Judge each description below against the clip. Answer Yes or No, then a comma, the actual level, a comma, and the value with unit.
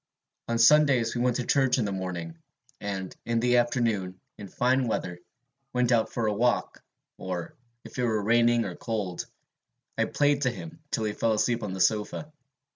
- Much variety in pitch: No, average, 3.5 semitones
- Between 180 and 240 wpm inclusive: Yes, average, 185 wpm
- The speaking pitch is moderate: No, low, 115 Hz